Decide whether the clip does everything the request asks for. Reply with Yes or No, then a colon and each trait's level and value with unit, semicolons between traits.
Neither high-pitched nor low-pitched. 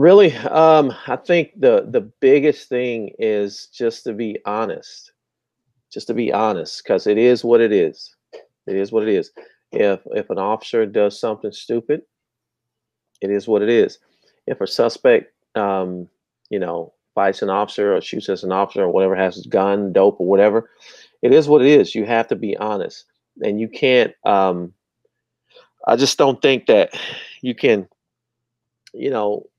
Yes: medium, 150 Hz